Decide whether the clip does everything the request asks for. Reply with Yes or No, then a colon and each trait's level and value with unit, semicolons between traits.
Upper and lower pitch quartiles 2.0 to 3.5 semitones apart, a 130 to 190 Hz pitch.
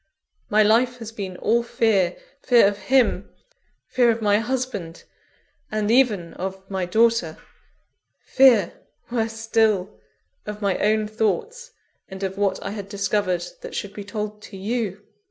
No: average, 2.8 semitones; high, 210 Hz